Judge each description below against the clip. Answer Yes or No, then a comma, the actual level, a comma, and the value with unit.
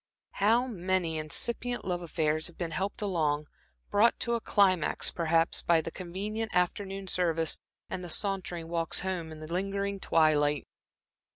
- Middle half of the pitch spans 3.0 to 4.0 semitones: Yes, average, 3.4 semitones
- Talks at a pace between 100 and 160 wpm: Yes, average, 150 wpm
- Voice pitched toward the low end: No, medium, 180 Hz